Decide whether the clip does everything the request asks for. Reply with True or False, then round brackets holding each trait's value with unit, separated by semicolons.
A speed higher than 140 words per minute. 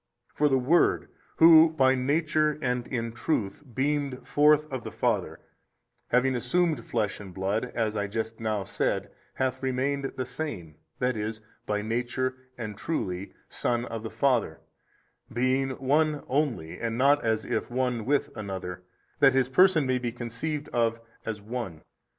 True (155 wpm)